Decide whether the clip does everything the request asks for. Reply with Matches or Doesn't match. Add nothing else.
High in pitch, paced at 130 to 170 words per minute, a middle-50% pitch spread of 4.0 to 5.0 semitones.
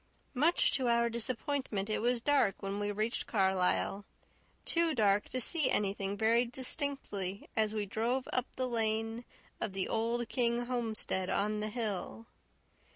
Doesn't match